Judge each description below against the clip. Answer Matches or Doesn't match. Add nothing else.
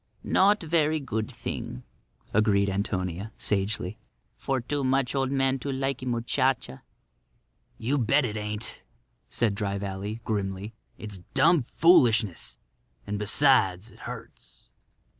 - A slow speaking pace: Matches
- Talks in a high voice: Doesn't match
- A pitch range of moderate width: Matches